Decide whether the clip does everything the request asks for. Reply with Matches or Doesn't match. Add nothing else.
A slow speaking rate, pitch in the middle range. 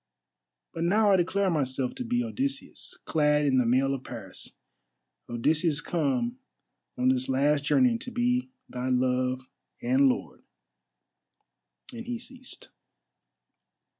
Matches